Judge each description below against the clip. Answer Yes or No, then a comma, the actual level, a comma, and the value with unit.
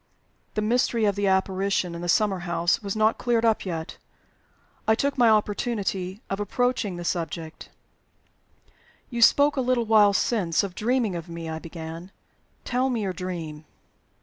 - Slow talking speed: No, average, 160 wpm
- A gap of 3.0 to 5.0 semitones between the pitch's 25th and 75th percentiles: Yes, average, 4.7 semitones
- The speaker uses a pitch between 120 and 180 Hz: No, high, 200 Hz